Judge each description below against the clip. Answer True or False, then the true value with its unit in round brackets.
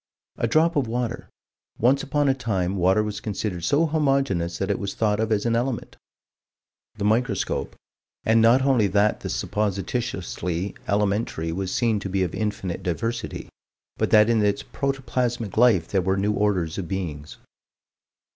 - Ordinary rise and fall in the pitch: True (3.8 semitones)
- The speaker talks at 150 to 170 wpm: True (160 wpm)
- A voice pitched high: False (105 Hz)